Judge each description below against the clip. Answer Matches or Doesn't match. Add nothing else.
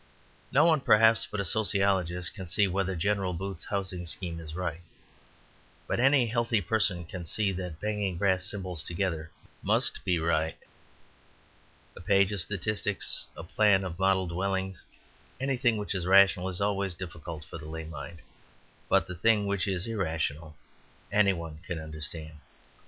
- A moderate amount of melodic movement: Matches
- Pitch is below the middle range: Matches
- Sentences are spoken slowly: Doesn't match